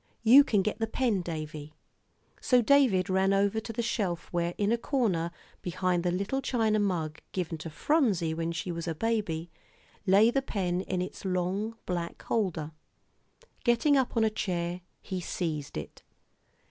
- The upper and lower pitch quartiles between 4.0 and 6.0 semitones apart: Yes, average, 4.7 semitones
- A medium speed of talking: Yes, average, 165 wpm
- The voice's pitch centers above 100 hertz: Yes, high, 190 Hz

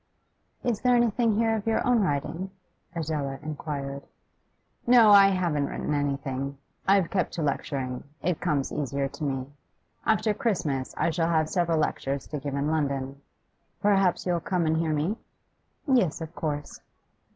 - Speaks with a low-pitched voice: No, medium, 160 Hz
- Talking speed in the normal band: Yes, average, 150 wpm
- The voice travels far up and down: Yes, wide, 5.7 semitones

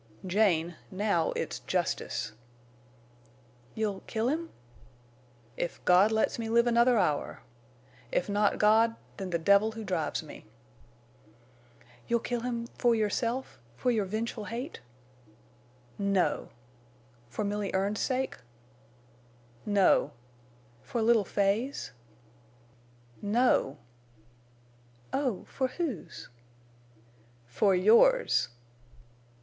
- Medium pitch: No, high, 215 Hz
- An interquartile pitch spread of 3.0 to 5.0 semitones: Yes, average, 3.4 semitones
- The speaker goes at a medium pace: No, slow, 85 wpm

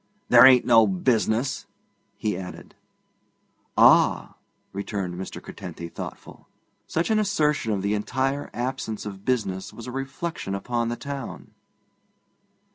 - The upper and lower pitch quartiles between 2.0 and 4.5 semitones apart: No, average, 5.2 semitones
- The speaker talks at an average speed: No, slow, 120 wpm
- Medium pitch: No, low, 115 Hz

